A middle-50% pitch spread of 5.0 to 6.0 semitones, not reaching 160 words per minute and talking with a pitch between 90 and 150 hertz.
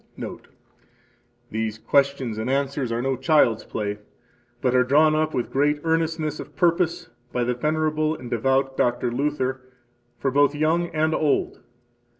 No: average, 3.8 semitones; average, 150 wpm; medium, 140 Hz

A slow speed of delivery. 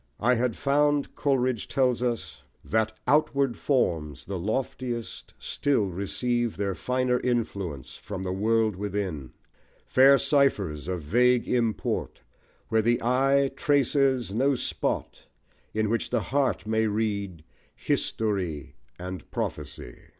Yes: slow, 120 wpm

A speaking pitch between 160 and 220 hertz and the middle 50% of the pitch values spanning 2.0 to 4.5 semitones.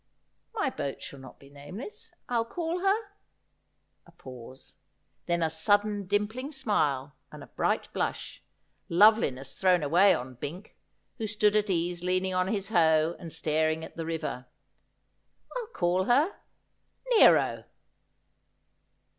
No: medium, 185 Hz; wide, 5.4 semitones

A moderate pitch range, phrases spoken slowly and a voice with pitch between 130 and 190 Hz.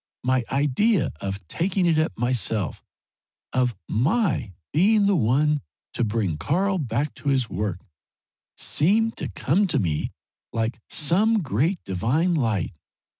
No: wide, 8.0 semitones; slow, 130 wpm; medium, 140 Hz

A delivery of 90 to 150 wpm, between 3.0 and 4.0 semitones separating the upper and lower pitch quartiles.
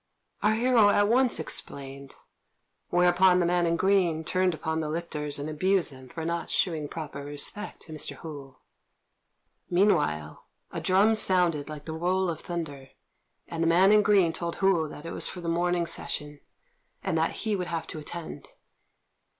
No: average, 170 wpm; average, 3.4 semitones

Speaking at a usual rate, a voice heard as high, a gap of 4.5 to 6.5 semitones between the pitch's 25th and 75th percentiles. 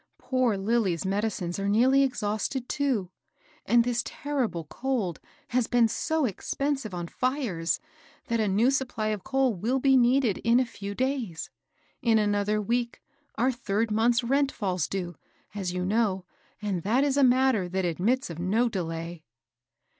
Yes: average, 160 wpm; high, 225 Hz; average, 5.0 semitones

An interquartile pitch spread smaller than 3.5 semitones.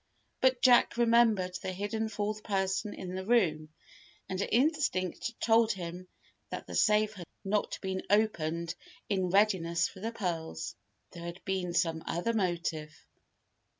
No: average, 3.9 semitones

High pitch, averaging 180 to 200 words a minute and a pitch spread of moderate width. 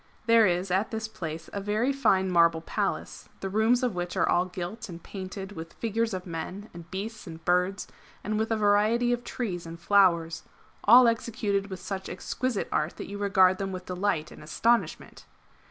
Yes: high, 195 Hz; average, 185 wpm; average, 3.8 semitones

